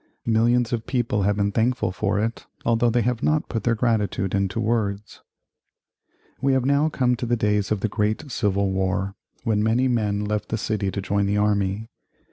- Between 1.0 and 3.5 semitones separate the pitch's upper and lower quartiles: Yes, average, 2.8 semitones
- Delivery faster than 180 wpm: Yes, average, 190 wpm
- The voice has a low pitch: Yes, low, 110 Hz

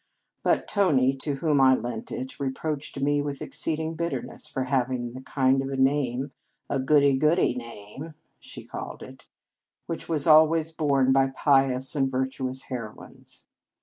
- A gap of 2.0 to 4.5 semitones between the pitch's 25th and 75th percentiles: Yes, narrow, 2.4 semitones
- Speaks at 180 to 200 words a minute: No, average, 160 wpm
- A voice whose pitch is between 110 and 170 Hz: Yes, low, 135 Hz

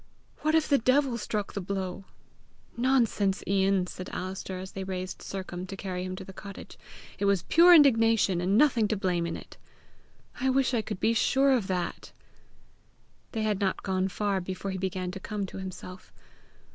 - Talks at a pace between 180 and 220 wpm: Yes, average, 185 wpm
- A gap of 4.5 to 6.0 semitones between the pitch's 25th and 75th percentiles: No, average, 3.4 semitones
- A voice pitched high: Yes, high, 195 Hz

